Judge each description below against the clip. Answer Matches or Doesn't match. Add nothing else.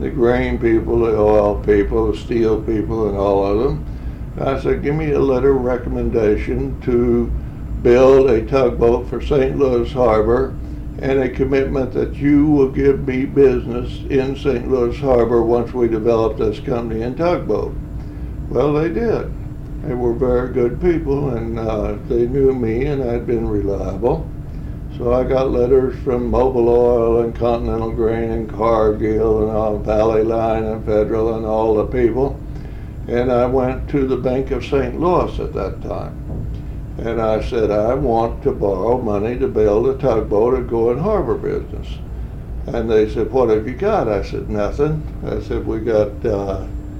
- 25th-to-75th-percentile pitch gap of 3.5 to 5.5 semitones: Doesn't match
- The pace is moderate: Matches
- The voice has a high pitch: Doesn't match